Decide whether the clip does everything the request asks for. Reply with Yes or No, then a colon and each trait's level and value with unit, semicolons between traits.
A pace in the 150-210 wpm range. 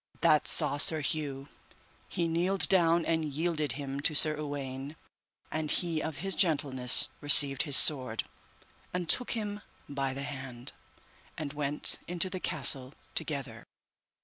No: average, 140 wpm